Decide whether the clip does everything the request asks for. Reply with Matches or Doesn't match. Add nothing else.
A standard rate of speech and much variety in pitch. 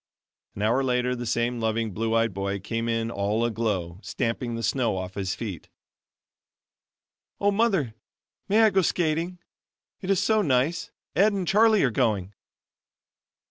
Matches